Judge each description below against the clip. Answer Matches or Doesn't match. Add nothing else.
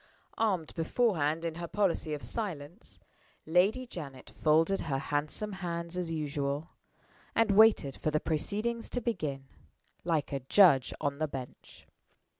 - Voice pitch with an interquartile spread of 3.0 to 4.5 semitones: Doesn't match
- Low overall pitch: Doesn't match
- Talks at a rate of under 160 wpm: Matches